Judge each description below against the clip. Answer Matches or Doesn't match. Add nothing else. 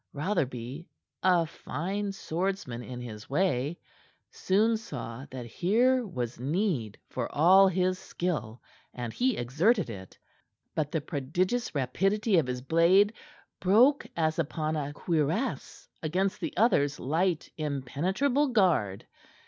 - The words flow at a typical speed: Doesn't match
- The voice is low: Doesn't match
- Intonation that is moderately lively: Doesn't match